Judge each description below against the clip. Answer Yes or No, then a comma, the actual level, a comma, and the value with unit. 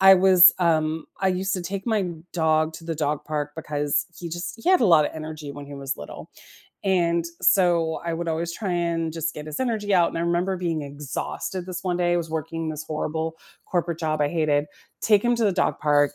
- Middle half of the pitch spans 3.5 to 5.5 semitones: No, average, 2.7 semitones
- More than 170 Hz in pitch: No, medium, 165 Hz